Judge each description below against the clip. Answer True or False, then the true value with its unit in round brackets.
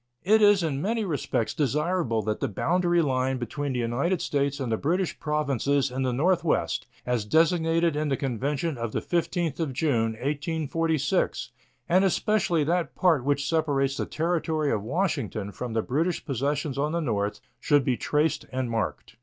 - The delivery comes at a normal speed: True (170 wpm)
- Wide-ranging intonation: False (4.5 semitones)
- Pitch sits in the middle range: True (145 Hz)